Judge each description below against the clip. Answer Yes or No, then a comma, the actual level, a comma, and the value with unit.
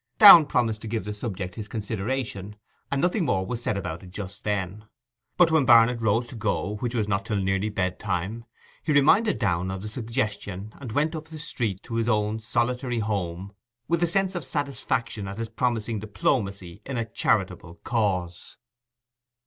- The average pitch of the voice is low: Yes, low, 110 Hz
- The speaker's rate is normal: Yes, average, 180 wpm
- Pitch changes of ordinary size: Yes, average, 4.0 semitones